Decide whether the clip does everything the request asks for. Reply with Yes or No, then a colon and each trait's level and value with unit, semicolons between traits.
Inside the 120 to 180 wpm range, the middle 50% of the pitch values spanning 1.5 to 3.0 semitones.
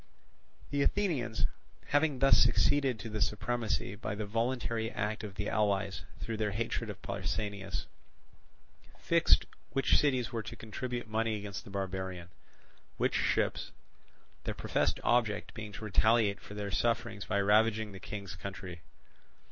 Yes: average, 140 wpm; average, 2.7 semitones